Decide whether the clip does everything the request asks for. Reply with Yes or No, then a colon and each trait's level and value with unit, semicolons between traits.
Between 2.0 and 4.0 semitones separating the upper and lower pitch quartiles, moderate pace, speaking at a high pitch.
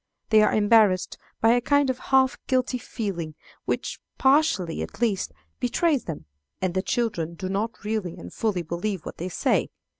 No: average, 5.2 semitones; average, 170 wpm; high, 215 Hz